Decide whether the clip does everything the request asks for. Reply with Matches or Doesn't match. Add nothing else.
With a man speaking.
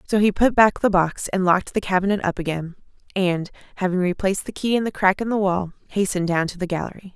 Doesn't match